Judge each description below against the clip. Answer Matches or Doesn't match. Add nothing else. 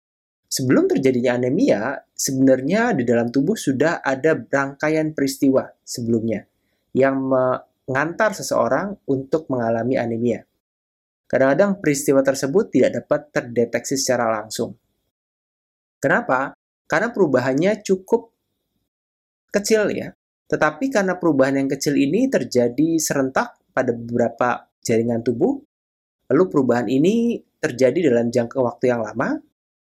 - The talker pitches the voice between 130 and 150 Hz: Matches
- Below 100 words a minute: Doesn't match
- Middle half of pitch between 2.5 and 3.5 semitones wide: Doesn't match